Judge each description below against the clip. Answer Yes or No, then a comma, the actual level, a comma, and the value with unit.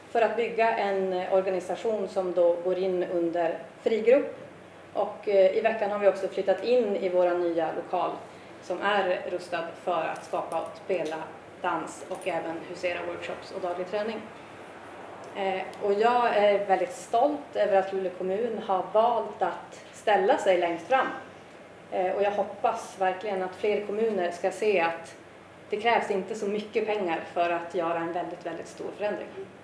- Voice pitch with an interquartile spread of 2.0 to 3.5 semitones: Yes, average, 2.8 semitones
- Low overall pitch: No, high, 190 Hz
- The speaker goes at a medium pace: Yes, average, 160 wpm